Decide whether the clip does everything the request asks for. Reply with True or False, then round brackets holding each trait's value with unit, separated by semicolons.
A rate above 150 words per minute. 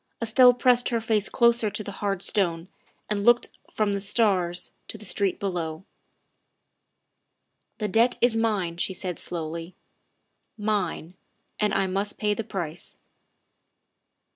False (140 wpm)